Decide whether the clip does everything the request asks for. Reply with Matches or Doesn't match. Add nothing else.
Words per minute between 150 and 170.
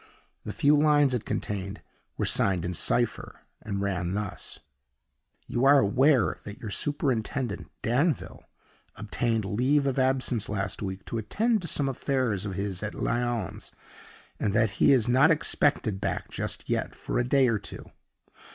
Matches